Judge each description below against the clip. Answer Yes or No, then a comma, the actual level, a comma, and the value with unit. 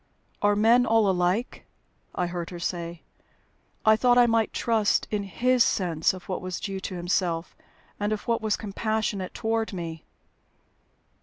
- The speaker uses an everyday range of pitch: Yes, average, 3.9 semitones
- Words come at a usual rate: Yes, average, 155 wpm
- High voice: Yes, high, 205 Hz